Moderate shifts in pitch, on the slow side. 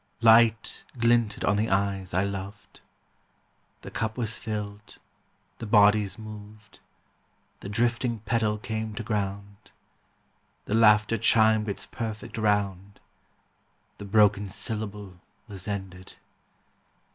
No: narrow, 1.7 semitones; slow, 110 wpm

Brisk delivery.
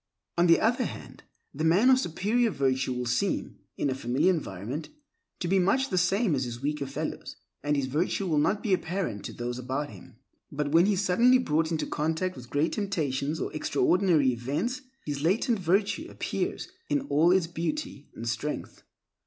No: average, 185 wpm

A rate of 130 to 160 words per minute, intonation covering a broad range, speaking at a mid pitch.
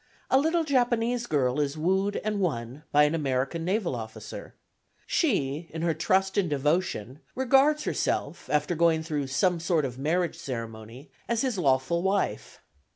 Yes: average, 155 wpm; wide, 6.7 semitones; medium, 165 Hz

